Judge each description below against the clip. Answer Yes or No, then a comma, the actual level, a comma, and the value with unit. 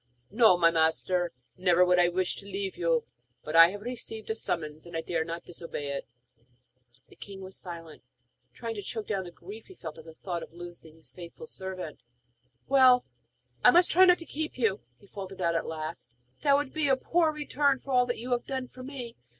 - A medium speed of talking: No, fast, 215 wpm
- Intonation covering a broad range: Yes, wide, 6.9 semitones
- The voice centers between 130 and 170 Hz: No, high, 190 Hz